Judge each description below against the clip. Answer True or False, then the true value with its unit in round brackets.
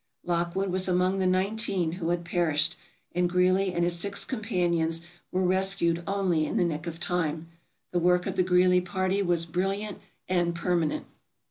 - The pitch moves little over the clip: True (1.6 semitones)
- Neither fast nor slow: True (165 wpm)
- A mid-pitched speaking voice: True (180 Hz)